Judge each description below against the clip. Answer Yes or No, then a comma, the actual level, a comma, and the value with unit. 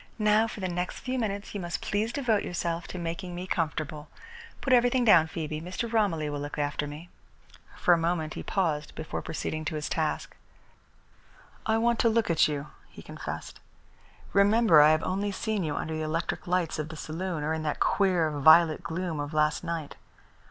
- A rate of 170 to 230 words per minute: Yes, average, 190 wpm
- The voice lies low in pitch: No, medium, 170 Hz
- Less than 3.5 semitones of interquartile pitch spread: No, average, 4.5 semitones